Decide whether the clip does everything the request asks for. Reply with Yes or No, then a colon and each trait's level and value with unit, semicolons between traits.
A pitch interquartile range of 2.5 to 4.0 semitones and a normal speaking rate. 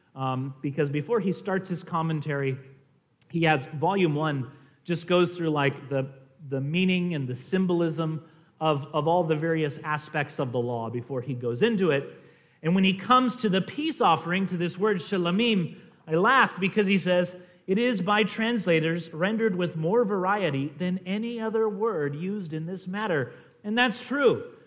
No: average, 4.7 semitones; average, 175 wpm